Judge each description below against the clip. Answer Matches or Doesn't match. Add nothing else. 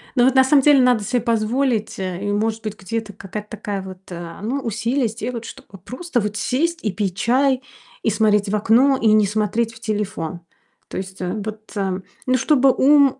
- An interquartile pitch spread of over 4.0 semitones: Doesn't match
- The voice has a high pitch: Matches